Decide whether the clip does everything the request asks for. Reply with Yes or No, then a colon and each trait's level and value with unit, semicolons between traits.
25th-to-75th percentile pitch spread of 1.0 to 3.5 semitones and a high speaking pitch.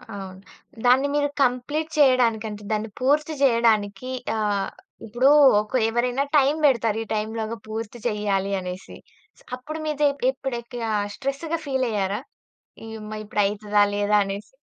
No: average, 4.1 semitones; high, 230 Hz